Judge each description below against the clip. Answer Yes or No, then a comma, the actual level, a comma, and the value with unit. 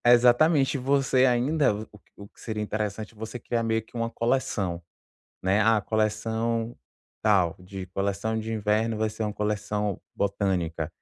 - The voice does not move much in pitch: Yes, narrow, 2.3 semitones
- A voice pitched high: No, low, 110 Hz